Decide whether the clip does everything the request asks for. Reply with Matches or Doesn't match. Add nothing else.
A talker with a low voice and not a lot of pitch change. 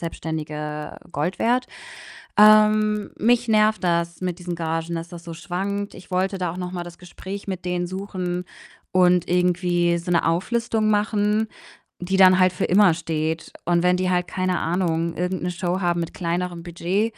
Doesn't match